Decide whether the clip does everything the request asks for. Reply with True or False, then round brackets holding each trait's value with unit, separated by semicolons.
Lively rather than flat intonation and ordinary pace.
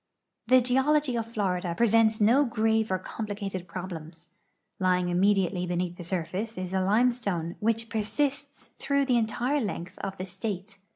False (4.1 semitones; 155 wpm)